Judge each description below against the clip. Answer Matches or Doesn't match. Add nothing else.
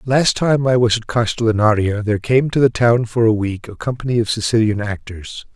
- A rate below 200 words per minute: Doesn't match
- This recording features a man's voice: Matches